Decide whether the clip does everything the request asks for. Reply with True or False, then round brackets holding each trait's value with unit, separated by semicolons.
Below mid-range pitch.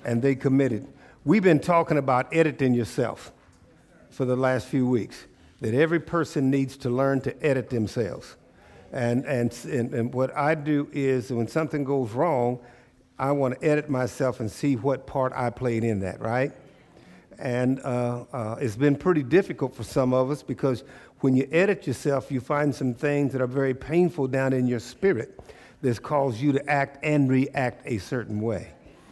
True (130 Hz)